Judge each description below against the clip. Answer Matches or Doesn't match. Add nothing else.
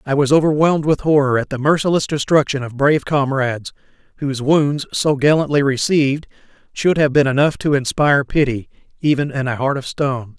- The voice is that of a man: Matches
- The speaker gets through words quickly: Doesn't match